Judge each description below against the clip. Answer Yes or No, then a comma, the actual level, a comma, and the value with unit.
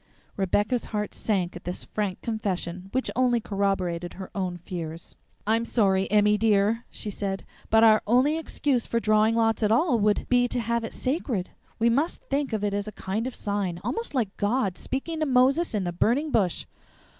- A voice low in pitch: No, high, 215 Hz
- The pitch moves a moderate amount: Yes, average, 3.9 semitones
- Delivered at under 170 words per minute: No, average, 190 wpm